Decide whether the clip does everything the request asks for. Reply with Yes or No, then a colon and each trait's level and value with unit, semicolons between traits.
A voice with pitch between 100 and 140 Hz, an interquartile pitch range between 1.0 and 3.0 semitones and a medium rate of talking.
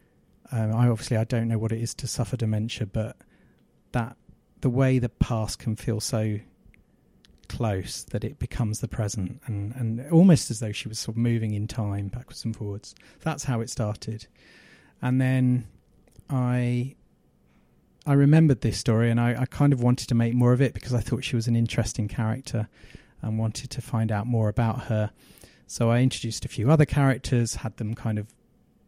Yes: low, 115 Hz; narrow, 2.4 semitones; average, 190 wpm